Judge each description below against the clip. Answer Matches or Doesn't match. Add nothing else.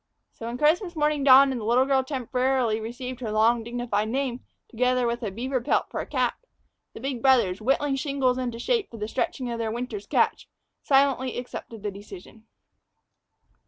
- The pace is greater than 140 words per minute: Matches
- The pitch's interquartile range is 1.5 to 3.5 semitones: Matches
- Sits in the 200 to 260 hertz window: Matches